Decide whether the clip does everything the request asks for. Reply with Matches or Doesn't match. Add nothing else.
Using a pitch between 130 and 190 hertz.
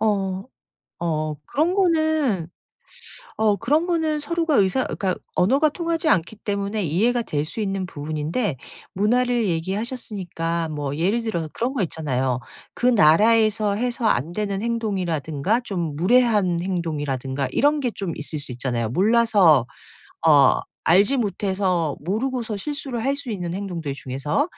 Doesn't match